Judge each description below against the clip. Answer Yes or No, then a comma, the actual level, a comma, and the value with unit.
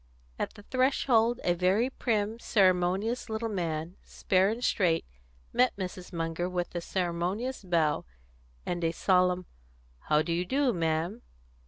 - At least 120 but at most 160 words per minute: Yes, average, 140 wpm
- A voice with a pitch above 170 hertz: Yes, medium, 185 Hz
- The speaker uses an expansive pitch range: No, average, 4.4 semitones